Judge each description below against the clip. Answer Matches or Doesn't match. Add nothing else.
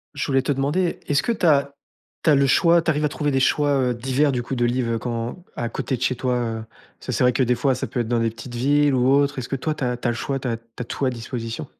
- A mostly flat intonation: Doesn't match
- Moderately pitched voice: Doesn't match